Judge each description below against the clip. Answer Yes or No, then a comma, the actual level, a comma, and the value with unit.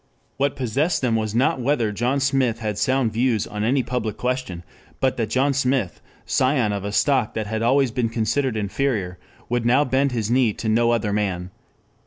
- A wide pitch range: No, average, 3.5 semitones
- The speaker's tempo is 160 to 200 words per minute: Yes, average, 190 wpm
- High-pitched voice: No, low, 120 Hz